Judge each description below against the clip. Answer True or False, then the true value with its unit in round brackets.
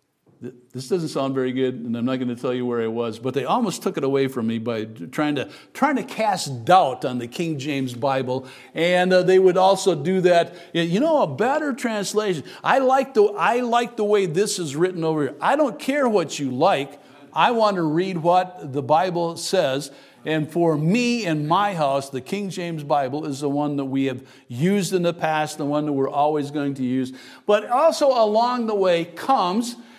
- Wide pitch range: True (6.0 semitones)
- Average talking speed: False (220 wpm)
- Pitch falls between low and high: True (160 Hz)